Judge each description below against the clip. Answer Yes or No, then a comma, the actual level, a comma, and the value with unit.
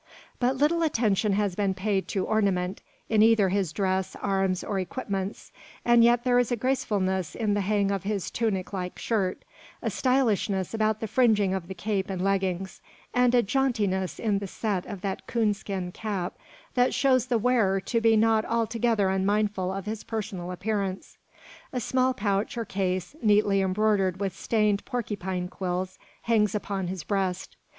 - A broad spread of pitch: No, average, 2.9 semitones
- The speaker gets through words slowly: No, average, 170 wpm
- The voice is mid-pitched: No, high, 205 Hz